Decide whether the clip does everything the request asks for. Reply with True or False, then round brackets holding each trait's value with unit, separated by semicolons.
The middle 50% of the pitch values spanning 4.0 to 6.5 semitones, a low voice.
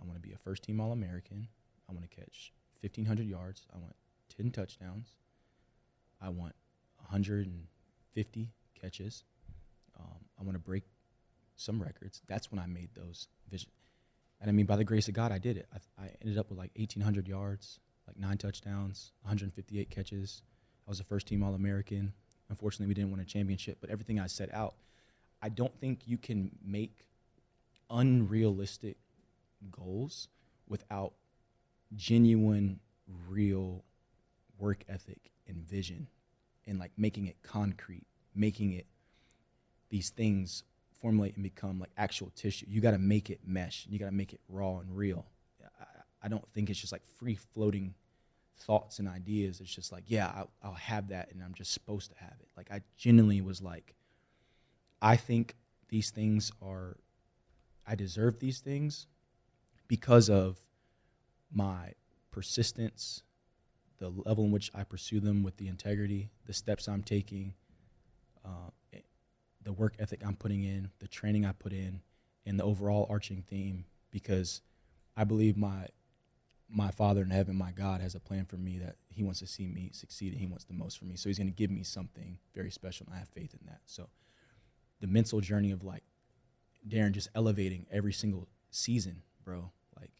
False (2.6 semitones; 100 Hz)